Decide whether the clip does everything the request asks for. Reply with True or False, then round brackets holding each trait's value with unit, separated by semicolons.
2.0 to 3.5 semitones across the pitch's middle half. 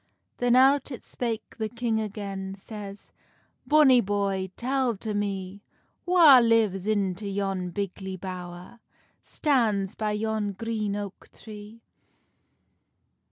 True (3.0 semitones)